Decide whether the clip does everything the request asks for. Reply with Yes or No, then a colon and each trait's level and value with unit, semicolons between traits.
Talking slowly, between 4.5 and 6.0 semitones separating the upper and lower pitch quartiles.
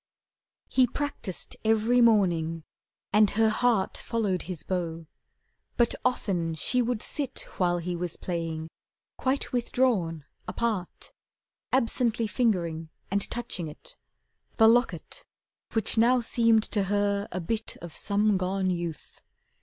Yes: slow, 120 wpm; average, 5.0 semitones